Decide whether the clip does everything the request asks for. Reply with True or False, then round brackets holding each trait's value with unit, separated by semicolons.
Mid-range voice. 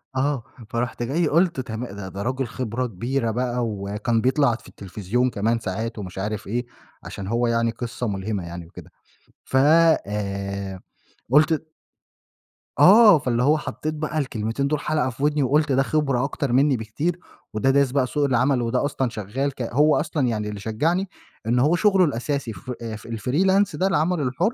False (125 Hz)